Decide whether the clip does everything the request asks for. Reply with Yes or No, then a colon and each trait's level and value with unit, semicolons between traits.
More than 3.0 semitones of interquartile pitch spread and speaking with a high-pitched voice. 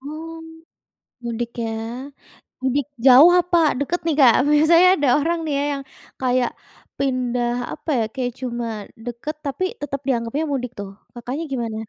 Yes: average, 3.9 semitones; very high, 265 Hz